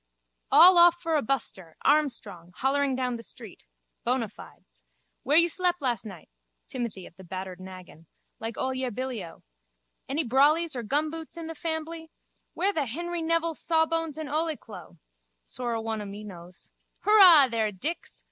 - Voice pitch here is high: Yes, very high, 265 Hz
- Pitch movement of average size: No, wide, 7.4 semitones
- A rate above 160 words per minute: No, average, 155 wpm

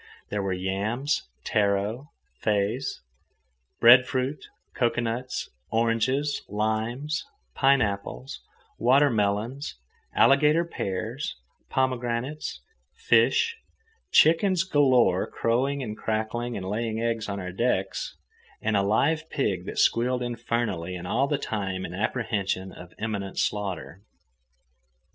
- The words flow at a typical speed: No, slow, 100 wpm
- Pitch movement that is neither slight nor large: Yes, average, 4.7 semitones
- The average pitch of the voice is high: No, low, 115 Hz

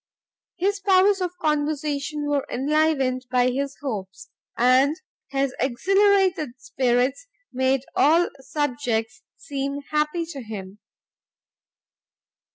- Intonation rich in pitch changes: No, average, 3.7 semitones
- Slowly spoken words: Yes, slow, 95 wpm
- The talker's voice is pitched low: No, very high, 280 Hz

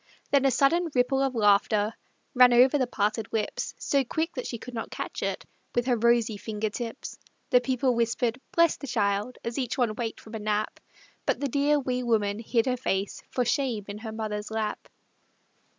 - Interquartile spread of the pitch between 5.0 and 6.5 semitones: No, average, 2.9 semitones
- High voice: Yes, high, 235 Hz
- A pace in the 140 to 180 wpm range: No, average, 195 wpm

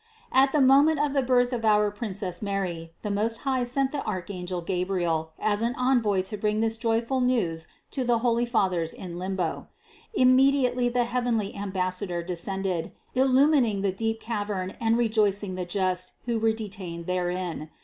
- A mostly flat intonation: No, average, 4.9 semitones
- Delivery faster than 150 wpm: Yes, average, 170 wpm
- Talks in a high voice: Yes, high, 210 Hz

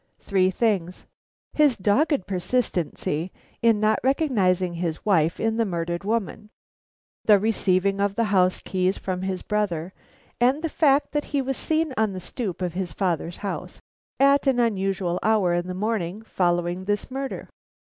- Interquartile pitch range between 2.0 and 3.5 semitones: No, average, 4.1 semitones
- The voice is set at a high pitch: Yes, high, 200 Hz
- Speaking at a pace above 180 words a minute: No, average, 155 wpm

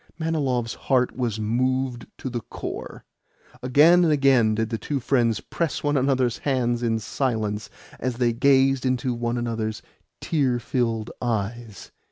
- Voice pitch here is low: Yes, low, 125 Hz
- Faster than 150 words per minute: No, average, 145 wpm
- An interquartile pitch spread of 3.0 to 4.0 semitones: No, narrow, 2.6 semitones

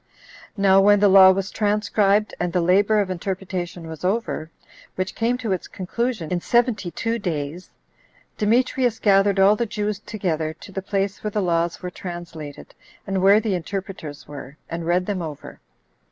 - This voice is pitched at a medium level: No, high, 195 Hz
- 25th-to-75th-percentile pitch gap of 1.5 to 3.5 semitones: Yes, average, 3.2 semitones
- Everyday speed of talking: Yes, average, 170 wpm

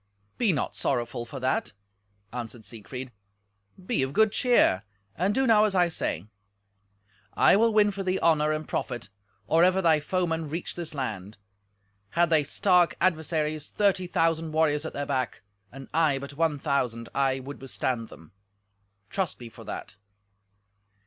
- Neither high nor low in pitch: Yes, medium, 150 Hz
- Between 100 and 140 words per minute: No, average, 155 wpm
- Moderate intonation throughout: No, wide, 6.0 semitones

